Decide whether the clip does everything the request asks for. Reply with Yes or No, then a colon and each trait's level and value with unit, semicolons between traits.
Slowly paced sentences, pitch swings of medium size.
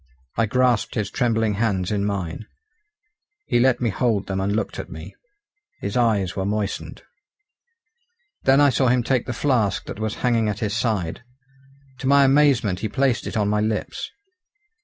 No: average, 170 wpm; average, 3.6 semitones